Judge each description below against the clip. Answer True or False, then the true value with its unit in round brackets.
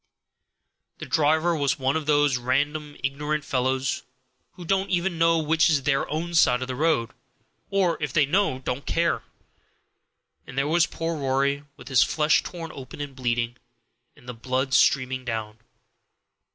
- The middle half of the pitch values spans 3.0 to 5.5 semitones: True (3.6 semitones)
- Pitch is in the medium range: True (145 Hz)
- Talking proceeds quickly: False (160 wpm)